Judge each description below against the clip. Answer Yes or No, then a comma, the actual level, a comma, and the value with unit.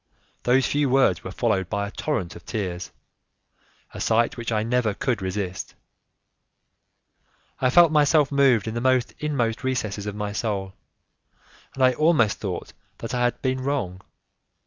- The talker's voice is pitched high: No, low, 120 Hz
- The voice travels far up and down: No, average, 4.4 semitones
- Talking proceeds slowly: No, average, 150 wpm